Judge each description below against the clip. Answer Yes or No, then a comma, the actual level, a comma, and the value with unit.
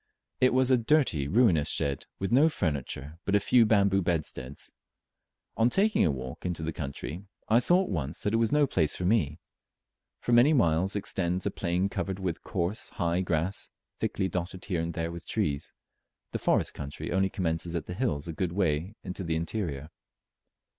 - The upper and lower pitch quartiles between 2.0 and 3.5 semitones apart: No, average, 4.7 semitones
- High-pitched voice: No, very low, 90 Hz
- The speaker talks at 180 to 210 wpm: Yes, average, 185 wpm